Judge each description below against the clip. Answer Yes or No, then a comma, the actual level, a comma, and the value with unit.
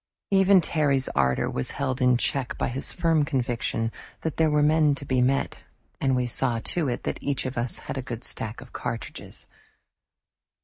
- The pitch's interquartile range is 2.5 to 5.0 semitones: Yes, average, 3.5 semitones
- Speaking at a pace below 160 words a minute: No, average, 185 wpm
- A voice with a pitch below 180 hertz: Yes, low, 135 Hz